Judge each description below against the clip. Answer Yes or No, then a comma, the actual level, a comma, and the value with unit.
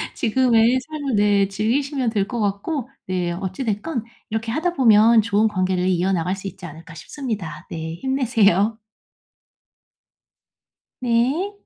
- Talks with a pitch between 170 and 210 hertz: No, high, 220 Hz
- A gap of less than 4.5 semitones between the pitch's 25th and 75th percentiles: No, average, 5.1 semitones